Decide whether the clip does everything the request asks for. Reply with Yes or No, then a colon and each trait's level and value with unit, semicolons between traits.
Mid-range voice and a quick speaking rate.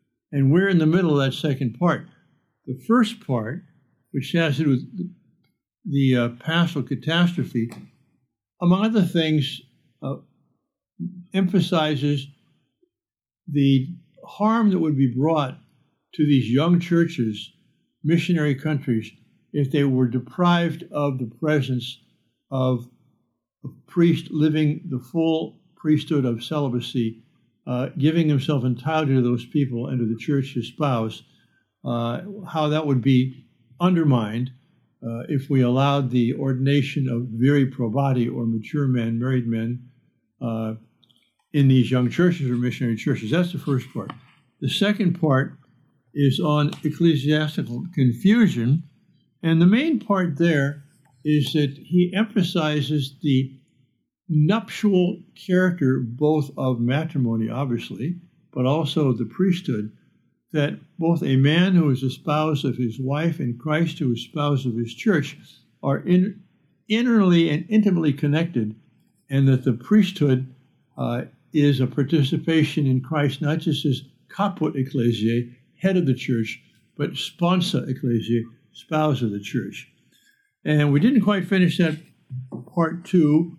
No: medium, 145 Hz; slow, 135 wpm